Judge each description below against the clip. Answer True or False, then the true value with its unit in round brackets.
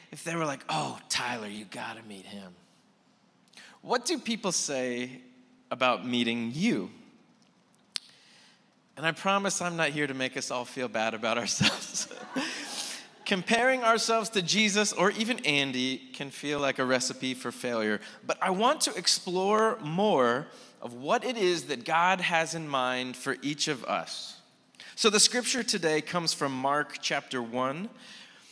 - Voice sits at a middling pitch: True (150 Hz)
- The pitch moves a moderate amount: False (8.5 semitones)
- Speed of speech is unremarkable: True (155 wpm)